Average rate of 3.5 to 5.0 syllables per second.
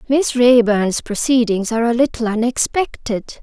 Yes: 4.6 syllables/s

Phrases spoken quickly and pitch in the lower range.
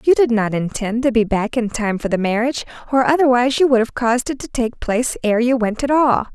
No: fast, 255 wpm; high, 240 Hz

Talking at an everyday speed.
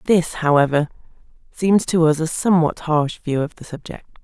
Yes: average, 170 wpm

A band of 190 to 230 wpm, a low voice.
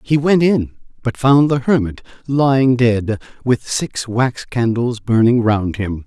No: average, 160 wpm; low, 120 Hz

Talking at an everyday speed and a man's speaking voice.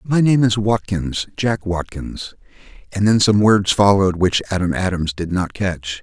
Yes: average, 160 wpm; male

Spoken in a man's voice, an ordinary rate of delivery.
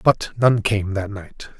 Yes: male; average, 190 wpm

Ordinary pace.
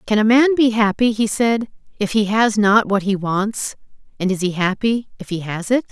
No: fast, 225 wpm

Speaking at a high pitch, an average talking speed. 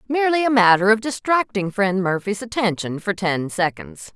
Yes: high, 205 Hz; average, 160 wpm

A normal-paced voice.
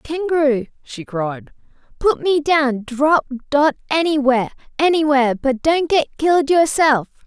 No: slow, 125 wpm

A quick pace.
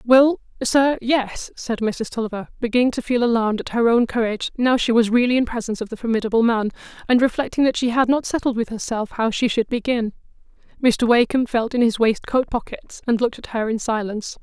Yes: fast, 210 wpm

